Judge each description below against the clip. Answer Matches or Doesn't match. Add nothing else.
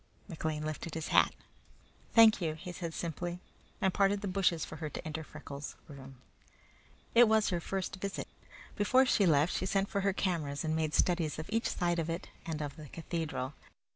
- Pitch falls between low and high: Matches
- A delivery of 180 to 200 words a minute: Matches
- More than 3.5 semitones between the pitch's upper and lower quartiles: Matches